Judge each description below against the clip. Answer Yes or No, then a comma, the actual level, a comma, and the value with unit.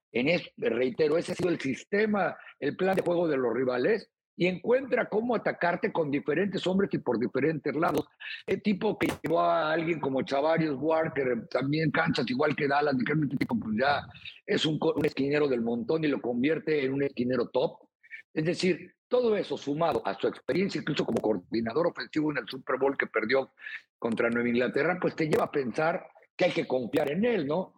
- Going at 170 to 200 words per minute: Yes, fast, 190 wpm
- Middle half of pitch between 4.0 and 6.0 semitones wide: Yes, average, 4.3 semitones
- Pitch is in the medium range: Yes, medium, 160 Hz